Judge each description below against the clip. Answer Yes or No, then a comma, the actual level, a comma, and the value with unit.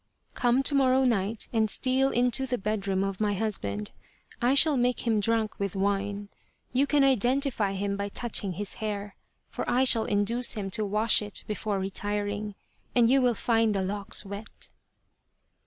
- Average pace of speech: Yes, average, 170 wpm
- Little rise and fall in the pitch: No, average, 3.5 semitones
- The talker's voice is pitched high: Yes, high, 215 Hz